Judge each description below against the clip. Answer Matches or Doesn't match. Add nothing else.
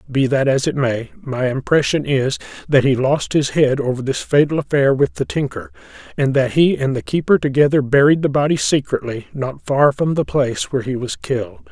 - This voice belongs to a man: Matches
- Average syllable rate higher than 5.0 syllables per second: Matches